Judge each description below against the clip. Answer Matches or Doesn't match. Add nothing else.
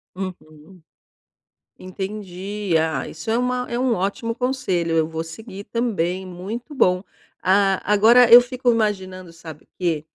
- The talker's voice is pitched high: Matches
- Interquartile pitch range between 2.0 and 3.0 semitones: Doesn't match